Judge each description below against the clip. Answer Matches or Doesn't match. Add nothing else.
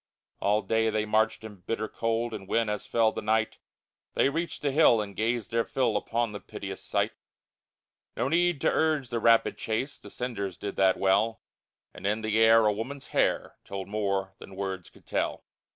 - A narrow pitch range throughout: Matches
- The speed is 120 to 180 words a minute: Doesn't match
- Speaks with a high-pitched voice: Doesn't match